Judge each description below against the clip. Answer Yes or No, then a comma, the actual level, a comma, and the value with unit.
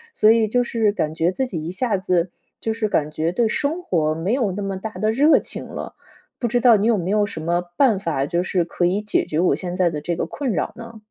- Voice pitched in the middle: No, high, 195 Hz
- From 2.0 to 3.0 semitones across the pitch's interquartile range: No, average, 4.9 semitones